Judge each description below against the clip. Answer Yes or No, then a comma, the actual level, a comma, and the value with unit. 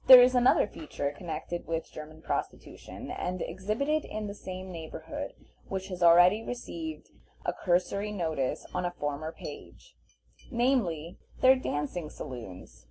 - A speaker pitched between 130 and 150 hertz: No, medium, 180 Hz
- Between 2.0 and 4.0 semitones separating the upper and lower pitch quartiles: No, average, 5.2 semitones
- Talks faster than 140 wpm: No, slow, 135 wpm